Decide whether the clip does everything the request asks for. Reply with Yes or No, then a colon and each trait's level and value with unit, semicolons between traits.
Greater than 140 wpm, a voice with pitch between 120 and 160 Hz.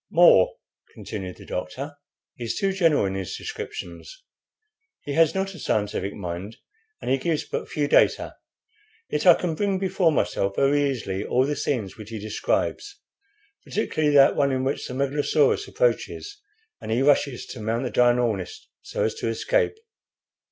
Yes: average, 160 wpm; medium, 140 Hz